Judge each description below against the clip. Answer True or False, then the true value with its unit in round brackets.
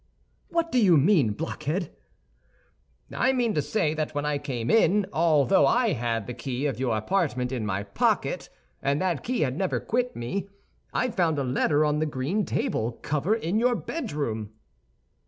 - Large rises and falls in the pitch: True (7.6 semitones)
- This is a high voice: False (150 Hz)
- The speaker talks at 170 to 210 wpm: True (175 wpm)